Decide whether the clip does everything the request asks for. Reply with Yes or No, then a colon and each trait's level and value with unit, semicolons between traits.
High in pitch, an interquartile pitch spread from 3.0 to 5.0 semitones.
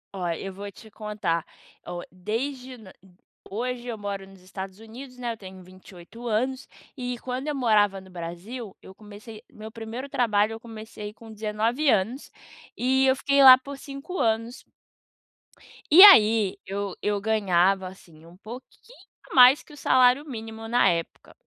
Yes: high, 220 Hz; average, 4.4 semitones